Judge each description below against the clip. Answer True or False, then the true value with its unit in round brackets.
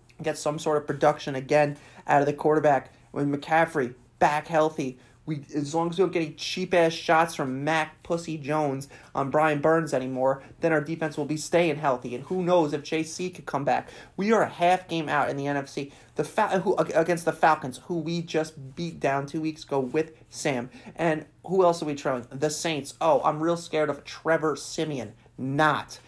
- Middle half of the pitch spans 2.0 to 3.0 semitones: True (2.7 semitones)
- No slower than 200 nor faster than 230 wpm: True (205 wpm)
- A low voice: False (155 Hz)